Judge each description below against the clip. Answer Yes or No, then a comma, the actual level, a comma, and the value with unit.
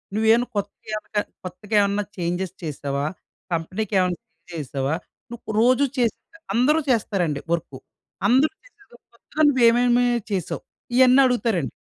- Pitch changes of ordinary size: No, wide, 6.4 semitones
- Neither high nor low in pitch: No, high, 210 Hz